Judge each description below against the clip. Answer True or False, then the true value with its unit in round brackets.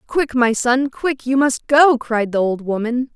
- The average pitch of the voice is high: True (250 Hz)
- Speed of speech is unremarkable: False (210 wpm)